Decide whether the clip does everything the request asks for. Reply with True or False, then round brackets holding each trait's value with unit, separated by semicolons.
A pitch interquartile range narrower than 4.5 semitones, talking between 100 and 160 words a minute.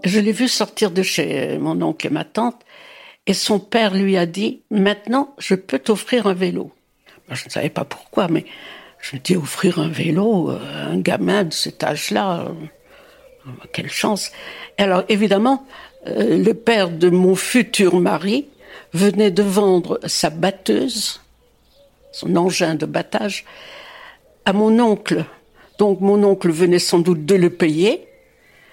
True (4.1 semitones; 150 wpm)